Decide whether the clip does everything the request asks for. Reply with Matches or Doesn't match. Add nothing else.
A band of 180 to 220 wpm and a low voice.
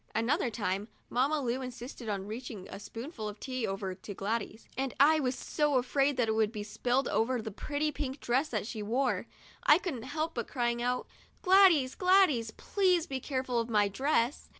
Doesn't match